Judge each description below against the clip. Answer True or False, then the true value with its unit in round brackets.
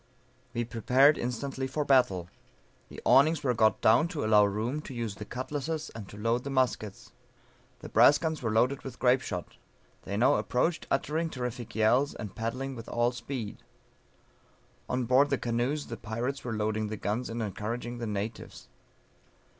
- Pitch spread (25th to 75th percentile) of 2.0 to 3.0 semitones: False (3.6 semitones)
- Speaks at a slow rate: False (170 wpm)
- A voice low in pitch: True (120 Hz)